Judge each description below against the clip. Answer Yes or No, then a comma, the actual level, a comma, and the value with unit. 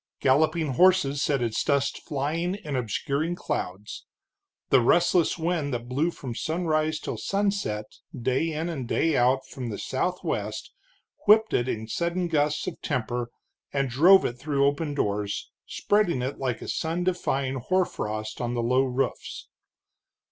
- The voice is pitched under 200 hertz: Yes, medium, 140 Hz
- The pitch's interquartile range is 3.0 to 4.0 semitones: No, average, 5.3 semitones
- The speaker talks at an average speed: Yes, average, 150 wpm